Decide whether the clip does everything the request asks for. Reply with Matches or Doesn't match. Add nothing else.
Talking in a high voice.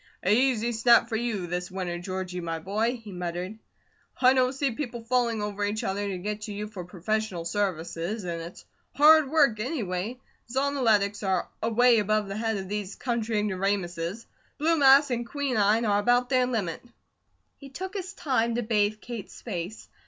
Matches